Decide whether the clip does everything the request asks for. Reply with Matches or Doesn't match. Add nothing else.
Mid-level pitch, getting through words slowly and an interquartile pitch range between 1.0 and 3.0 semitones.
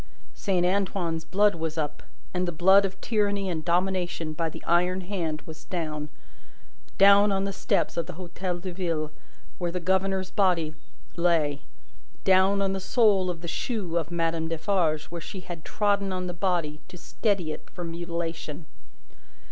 Doesn't match